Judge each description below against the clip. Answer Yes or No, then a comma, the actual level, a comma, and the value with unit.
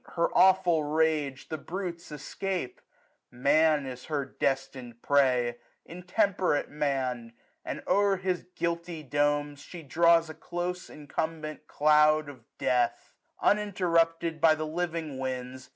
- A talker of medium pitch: Yes, medium, 155 Hz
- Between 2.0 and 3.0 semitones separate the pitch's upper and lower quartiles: No, average, 3.6 semitones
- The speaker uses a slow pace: Yes, slow, 125 wpm